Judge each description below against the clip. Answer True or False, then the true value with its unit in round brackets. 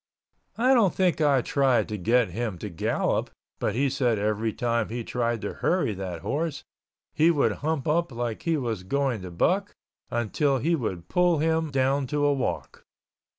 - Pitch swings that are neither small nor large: False (5.8 semitones)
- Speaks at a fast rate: False (180 wpm)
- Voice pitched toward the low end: True (130 Hz)